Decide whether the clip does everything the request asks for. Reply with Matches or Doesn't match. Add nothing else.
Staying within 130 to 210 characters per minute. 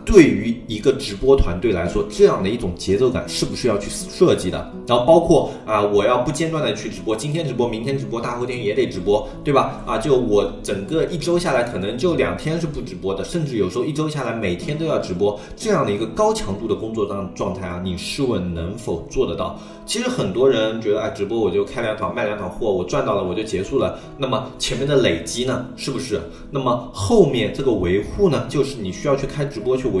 Doesn't match